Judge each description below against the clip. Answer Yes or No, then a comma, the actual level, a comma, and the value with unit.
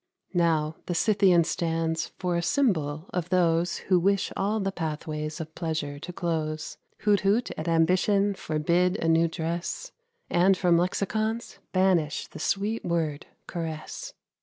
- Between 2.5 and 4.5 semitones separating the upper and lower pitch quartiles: Yes, average, 3.2 semitones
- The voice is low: No, medium, 170 Hz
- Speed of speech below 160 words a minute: Yes, average, 140 wpm